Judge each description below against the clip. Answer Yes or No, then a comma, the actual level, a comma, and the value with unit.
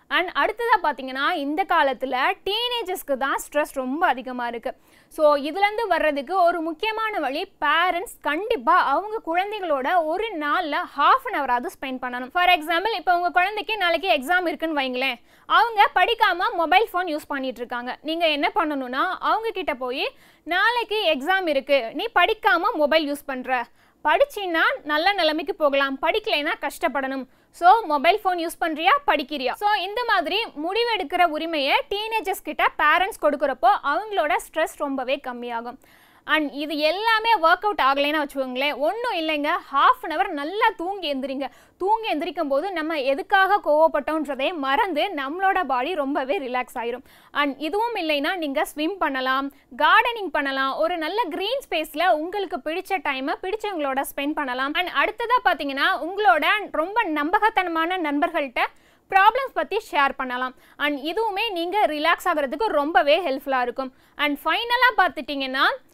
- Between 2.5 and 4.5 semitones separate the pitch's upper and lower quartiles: No, average, 5.0 semitones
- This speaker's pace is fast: Yes, fast, 135 wpm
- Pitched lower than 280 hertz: No, very high, 330 Hz